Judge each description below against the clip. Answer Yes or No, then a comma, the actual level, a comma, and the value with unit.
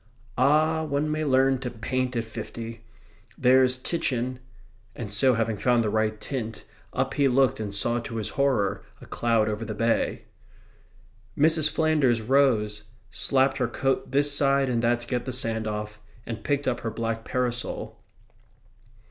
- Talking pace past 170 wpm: No, average, 160 wpm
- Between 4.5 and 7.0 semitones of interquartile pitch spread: No, average, 3.2 semitones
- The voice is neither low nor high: No, low, 125 Hz